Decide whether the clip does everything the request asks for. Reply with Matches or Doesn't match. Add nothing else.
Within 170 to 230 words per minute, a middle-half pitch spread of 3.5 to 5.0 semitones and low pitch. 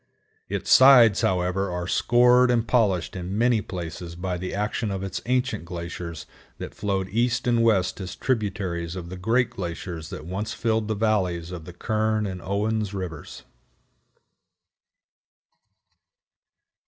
Doesn't match